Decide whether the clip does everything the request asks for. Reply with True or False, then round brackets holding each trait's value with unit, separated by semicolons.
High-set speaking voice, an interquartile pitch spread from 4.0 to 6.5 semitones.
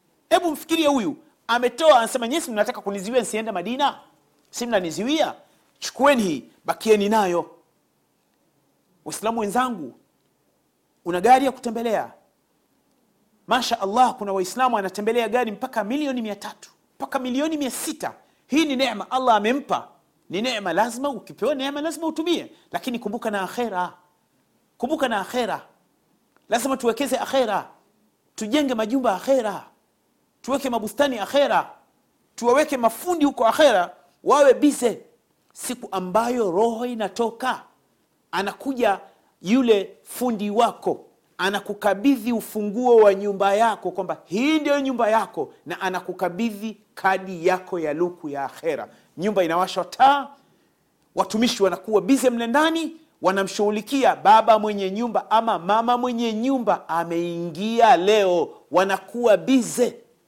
True (230 Hz; 5.0 semitones)